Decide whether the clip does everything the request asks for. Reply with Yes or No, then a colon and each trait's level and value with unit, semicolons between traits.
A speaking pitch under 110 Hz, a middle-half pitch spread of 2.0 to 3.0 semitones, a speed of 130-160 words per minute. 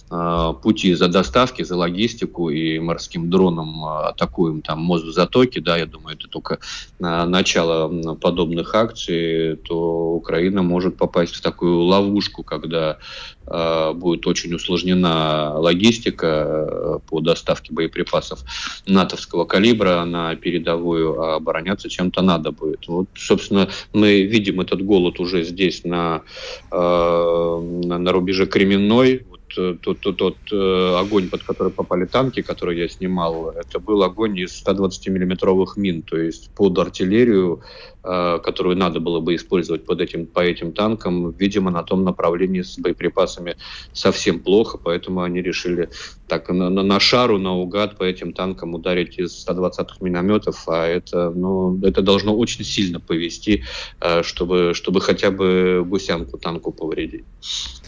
Yes: very low, 90 Hz; narrow, 2.4 semitones; average, 135 wpm